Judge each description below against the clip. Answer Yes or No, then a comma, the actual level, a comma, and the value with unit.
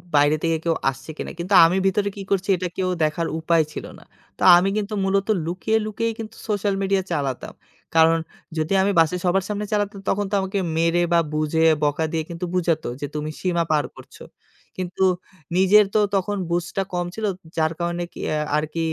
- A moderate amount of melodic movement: Yes, average, 3.3 semitones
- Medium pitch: Yes, medium, 175 Hz